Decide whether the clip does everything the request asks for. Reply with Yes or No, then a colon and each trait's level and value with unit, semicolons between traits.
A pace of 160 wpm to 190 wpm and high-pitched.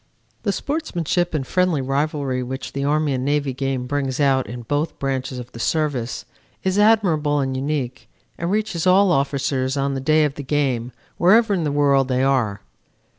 No: average, 180 wpm; medium, 140 Hz